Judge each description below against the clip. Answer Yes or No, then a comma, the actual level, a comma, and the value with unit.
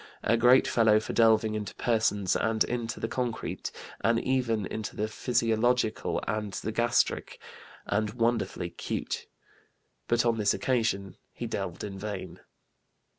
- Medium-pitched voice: No, low, 110 Hz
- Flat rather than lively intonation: Yes, narrow, 1.8 semitones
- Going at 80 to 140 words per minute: Yes, slow, 135 wpm